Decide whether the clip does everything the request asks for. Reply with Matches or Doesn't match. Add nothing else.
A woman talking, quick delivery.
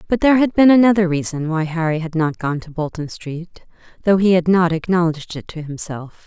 Matches